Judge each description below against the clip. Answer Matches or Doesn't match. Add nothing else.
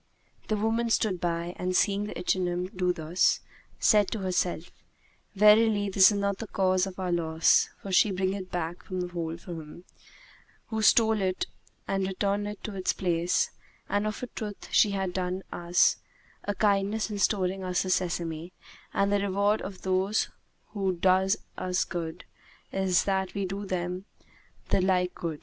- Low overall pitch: Doesn't match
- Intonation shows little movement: Matches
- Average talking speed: Matches